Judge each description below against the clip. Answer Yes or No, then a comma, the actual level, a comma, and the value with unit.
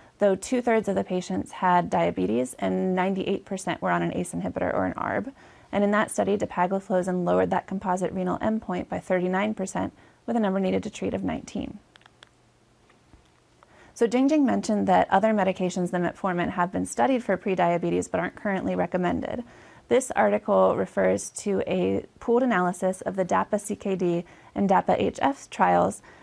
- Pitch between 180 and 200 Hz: Yes, medium, 185 Hz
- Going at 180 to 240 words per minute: No, average, 160 wpm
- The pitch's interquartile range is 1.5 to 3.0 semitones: Yes, narrow, 2.5 semitones